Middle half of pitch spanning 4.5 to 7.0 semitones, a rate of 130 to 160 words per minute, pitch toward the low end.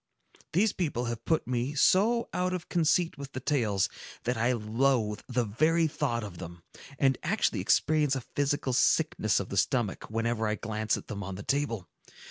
No: wide, 5.4 semitones; average, 180 wpm; low, 125 Hz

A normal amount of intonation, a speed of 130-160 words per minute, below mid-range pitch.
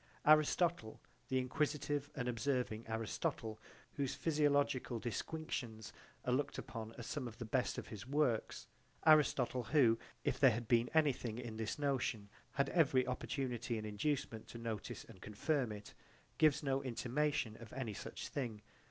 Yes: average, 4.1 semitones; average, 150 wpm; low, 125 Hz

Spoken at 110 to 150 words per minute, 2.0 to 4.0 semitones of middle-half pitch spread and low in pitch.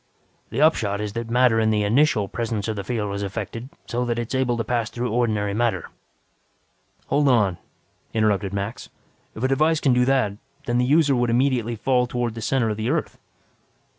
No: average, 200 wpm; average, 2.9 semitones; low, 120 Hz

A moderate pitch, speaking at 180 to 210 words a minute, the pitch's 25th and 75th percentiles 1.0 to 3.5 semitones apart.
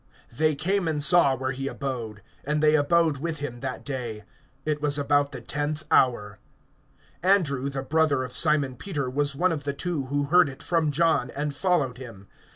Yes: medium, 145 Hz; average, 185 wpm; average, 2.9 semitones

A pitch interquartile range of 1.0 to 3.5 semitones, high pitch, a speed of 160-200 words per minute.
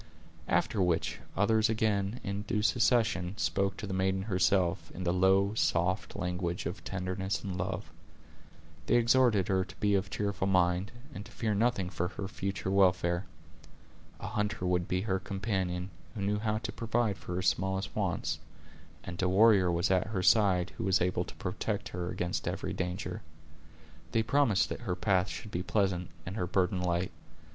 No: narrow, 2.4 semitones; very low, 95 Hz; average, 175 wpm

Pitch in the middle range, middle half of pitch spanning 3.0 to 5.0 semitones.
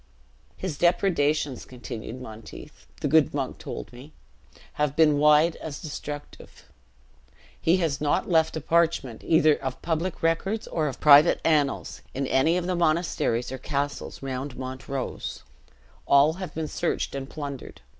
Yes: medium, 150 Hz; average, 3.3 semitones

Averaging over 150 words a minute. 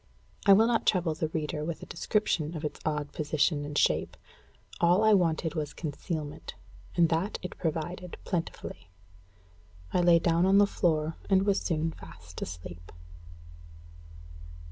No: average, 145 wpm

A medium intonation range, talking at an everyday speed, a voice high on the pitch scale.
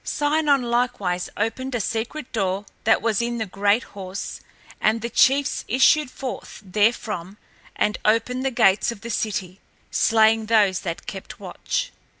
Yes: average, 3.8 semitones; average, 150 wpm; high, 225 Hz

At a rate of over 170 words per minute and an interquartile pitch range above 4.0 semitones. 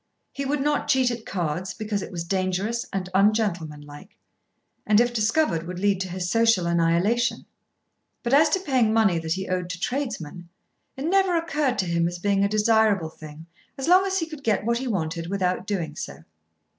Yes: average, 190 wpm; wide, 5.5 semitones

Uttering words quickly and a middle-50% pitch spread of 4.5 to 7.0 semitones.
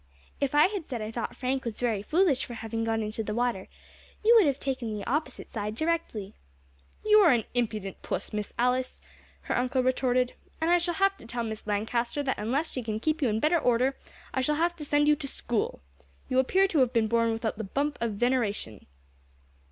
Yes: fast, 215 wpm; average, 4.8 semitones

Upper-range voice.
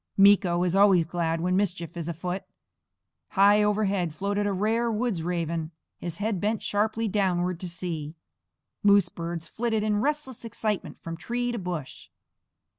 Yes: high, 195 Hz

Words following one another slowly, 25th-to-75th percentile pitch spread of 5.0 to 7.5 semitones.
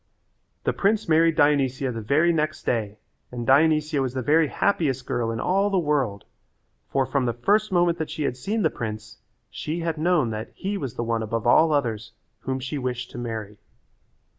No: average, 190 wpm; wide, 5.5 semitones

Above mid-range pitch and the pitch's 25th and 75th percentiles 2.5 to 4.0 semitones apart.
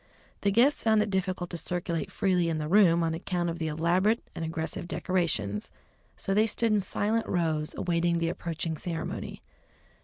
No: medium, 175 Hz; average, 2.9 semitones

